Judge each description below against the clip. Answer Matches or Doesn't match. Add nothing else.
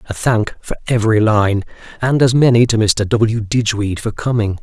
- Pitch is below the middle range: Matches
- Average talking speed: Matches